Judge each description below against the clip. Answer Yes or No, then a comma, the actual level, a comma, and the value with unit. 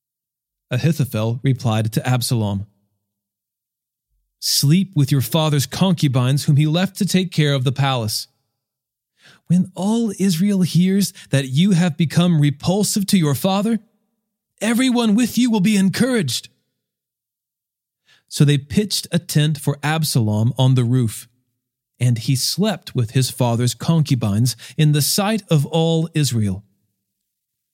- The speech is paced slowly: Yes, slow, 130 wpm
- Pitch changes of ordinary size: No, wide, 6.8 semitones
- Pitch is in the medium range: Yes, medium, 145 Hz